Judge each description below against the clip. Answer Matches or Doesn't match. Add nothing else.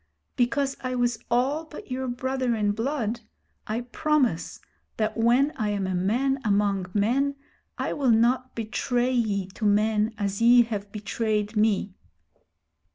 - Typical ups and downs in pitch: Matches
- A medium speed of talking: Matches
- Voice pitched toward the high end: Matches